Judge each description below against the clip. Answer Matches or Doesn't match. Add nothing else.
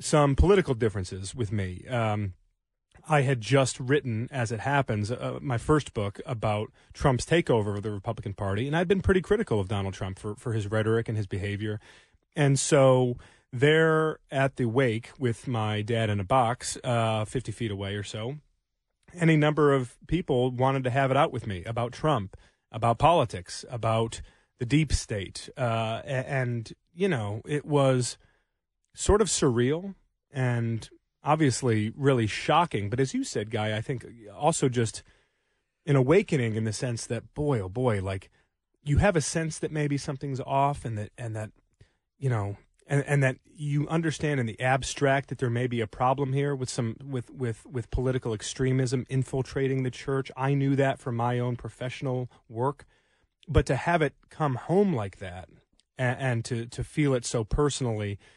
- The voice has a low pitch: Matches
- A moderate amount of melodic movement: Matches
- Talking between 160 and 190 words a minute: Matches